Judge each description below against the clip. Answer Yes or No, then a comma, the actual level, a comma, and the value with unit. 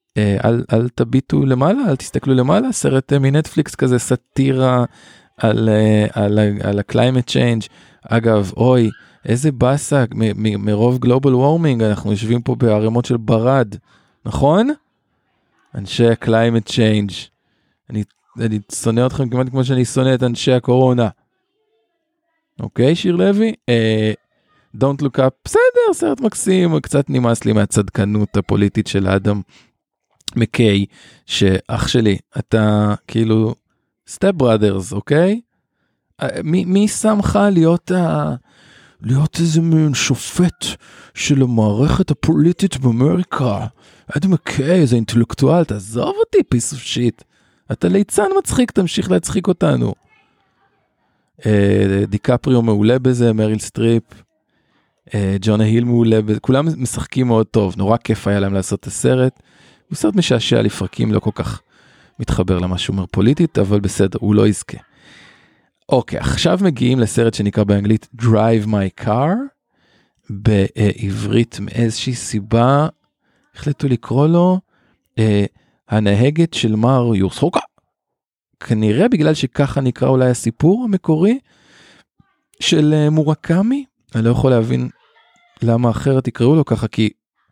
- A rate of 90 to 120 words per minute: Yes, average, 115 wpm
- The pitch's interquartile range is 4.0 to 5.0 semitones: No, wide, 5.5 semitones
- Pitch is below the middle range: Yes, low, 120 Hz